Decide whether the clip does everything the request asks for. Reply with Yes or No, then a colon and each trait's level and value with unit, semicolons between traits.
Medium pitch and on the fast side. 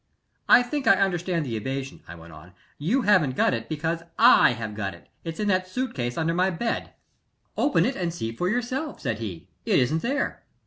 Yes: medium, 165 Hz; fast, 210 wpm